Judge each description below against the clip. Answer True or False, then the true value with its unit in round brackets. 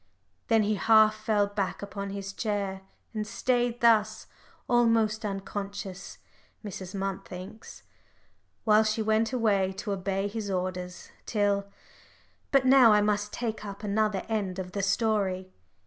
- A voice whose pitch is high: True (205 Hz)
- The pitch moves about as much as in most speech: False (2.0 semitones)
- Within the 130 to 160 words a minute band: True (135 wpm)